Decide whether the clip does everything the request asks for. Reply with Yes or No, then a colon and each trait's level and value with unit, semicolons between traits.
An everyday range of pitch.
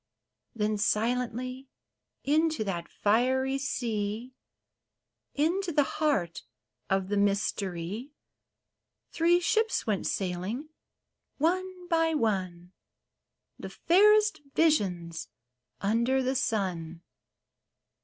No: wide, 7.8 semitones